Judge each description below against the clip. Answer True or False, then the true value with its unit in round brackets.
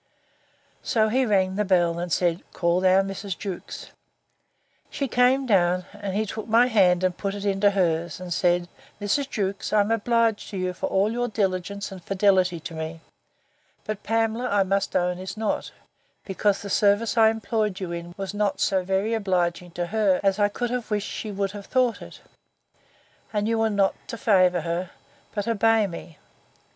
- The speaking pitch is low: False (200 Hz)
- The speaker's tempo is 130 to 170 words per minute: False (185 wpm)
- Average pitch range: True (3.0 semitones)